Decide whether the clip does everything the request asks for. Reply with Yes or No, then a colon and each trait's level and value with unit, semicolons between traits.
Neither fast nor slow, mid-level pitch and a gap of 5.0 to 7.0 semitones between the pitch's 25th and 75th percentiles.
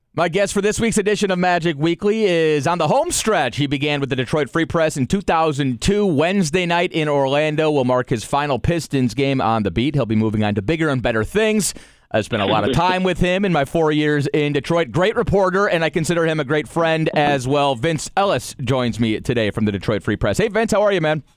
No: fast, 240 wpm; medium, 155 Hz; average, 5.3 semitones